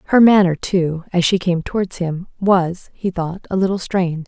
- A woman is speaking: Yes, female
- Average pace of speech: Yes, average, 195 wpm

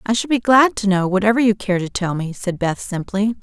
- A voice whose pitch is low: No, high, 205 Hz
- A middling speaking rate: No, fast, 265 wpm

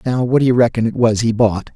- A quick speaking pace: Yes, fast, 305 wpm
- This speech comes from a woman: No, male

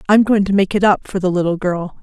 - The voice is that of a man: No, female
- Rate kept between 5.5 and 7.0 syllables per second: Yes, 6.0 syllables/s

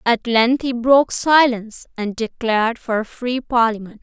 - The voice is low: No, high, 235 Hz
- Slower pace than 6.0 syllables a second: Yes, 4.7 syllables/s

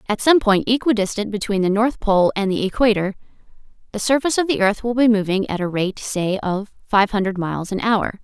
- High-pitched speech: Yes, high, 210 Hz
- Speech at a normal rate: No, fast, 210 wpm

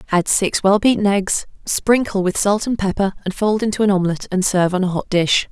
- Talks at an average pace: No, fast, 230 wpm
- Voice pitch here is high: Yes, high, 195 Hz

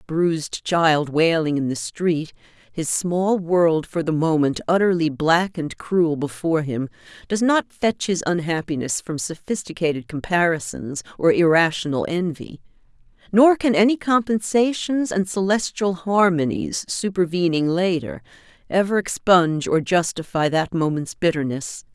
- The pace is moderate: No, slow, 125 wpm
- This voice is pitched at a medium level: Yes, medium, 170 Hz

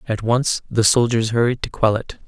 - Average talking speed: No, fast, 210 wpm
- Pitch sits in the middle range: No, low, 115 Hz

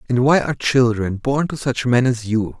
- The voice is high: No, low, 125 Hz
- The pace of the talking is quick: Yes, fast, 230 wpm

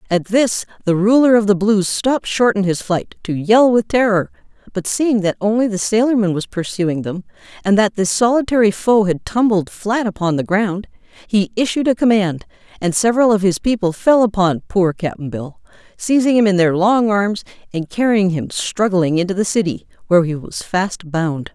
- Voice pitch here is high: Yes, high, 200 Hz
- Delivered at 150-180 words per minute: No, average, 190 wpm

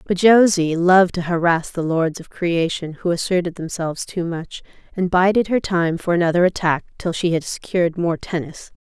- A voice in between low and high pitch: Yes, medium, 175 Hz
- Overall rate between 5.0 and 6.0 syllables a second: Yes, 5.2 syllables/s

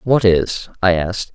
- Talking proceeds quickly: No, average, 180 wpm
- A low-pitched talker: Yes, very low, 95 Hz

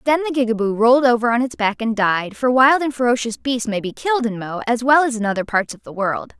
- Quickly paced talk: Yes, fast, 270 wpm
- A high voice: Yes, high, 235 Hz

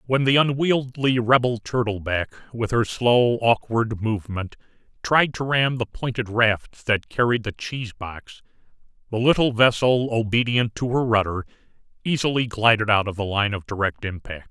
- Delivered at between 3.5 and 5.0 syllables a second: Yes, 4.7 syllables/s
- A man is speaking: Yes, male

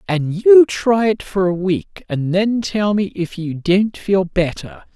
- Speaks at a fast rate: No, average, 195 wpm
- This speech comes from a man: Yes, male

